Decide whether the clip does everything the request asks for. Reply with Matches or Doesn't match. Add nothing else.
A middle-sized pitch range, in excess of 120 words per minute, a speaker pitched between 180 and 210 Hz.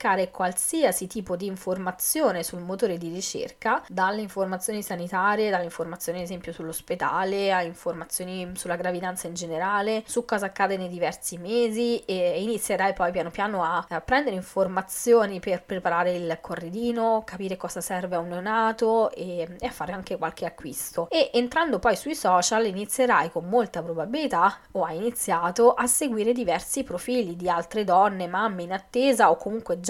Matches